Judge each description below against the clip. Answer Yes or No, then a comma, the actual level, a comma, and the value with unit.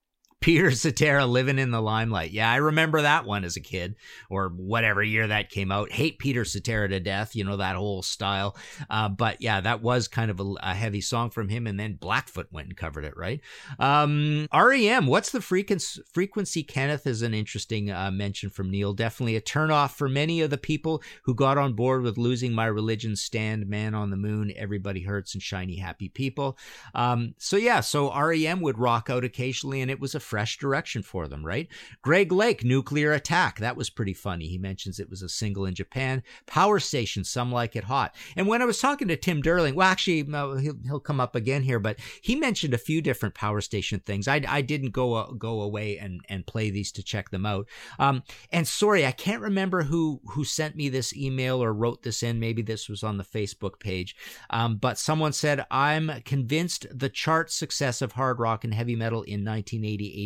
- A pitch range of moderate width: No, wide, 5.9 semitones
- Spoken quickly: Yes, fast, 210 wpm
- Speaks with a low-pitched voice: Yes, low, 120 Hz